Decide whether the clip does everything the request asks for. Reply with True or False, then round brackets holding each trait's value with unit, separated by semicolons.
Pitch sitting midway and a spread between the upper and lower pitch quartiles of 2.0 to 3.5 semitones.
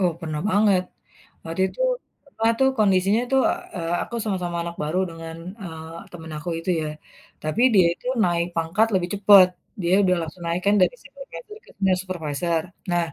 True (175 Hz; 3.1 semitones)